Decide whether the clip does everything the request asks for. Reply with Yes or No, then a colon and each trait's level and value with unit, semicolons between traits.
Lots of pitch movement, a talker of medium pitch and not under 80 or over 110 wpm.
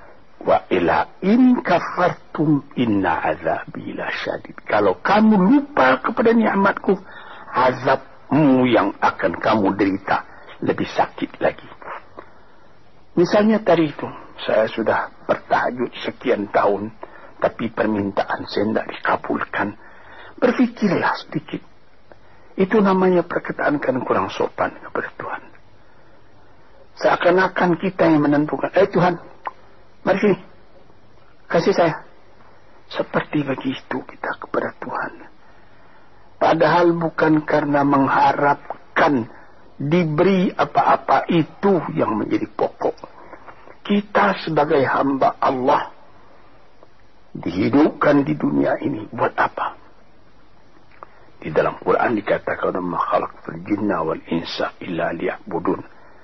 Yes: wide, 6.5 semitones; medium, 175 Hz; average, 95 wpm